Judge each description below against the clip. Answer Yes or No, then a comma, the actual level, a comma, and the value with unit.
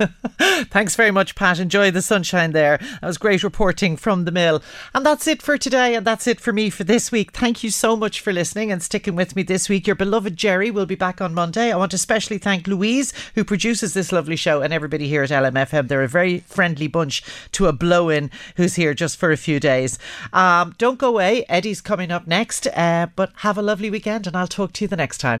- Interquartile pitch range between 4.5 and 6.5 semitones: No, average, 4.0 semitones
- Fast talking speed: Yes, fast, 240 wpm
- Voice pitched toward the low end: No, high, 195 Hz